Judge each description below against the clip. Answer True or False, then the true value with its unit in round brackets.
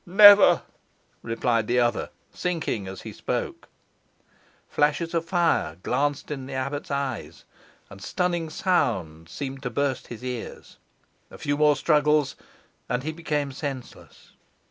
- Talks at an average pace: False (130 wpm)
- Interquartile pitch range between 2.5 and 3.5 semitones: False (3.9 semitones)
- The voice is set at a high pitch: False (140 Hz)